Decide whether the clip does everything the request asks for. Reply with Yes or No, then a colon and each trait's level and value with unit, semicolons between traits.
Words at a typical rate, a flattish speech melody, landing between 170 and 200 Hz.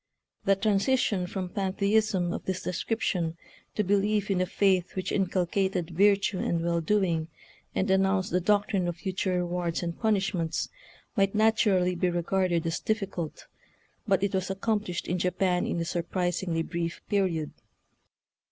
Yes: average, 150 wpm; narrow, 2.3 semitones; medium, 185 Hz